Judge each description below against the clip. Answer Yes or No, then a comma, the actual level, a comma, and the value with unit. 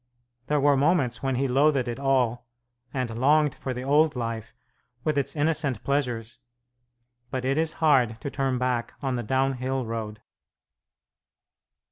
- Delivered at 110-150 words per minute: Yes, average, 145 wpm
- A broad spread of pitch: No, average, 2.8 semitones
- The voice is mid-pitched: No, low, 130 Hz